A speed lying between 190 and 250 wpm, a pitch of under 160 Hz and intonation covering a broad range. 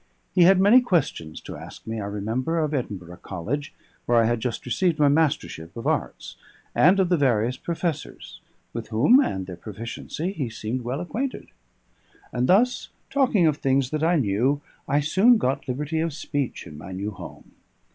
No: average, 175 wpm; medium, 140 Hz; wide, 7.1 semitones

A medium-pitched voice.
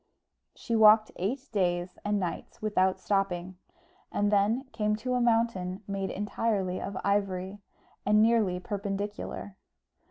No: high, 205 Hz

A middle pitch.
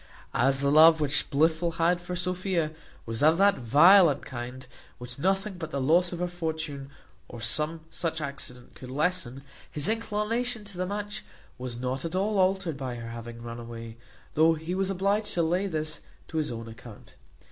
Yes: medium, 160 Hz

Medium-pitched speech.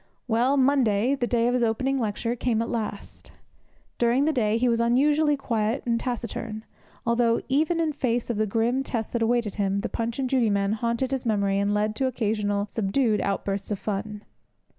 No: high, 230 Hz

